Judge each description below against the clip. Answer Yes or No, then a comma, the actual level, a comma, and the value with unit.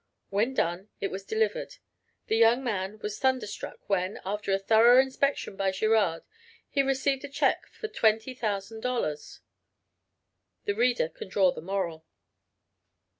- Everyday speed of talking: No, slow, 130 wpm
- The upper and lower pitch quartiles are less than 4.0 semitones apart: No, average, 4.7 semitones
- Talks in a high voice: Yes, high, 215 Hz